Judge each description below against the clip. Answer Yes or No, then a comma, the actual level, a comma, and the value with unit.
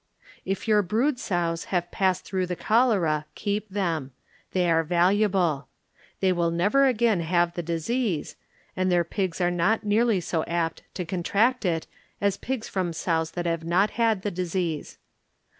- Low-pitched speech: No, medium, 180 Hz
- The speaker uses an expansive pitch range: No, average, 3.6 semitones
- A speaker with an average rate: Yes, average, 160 wpm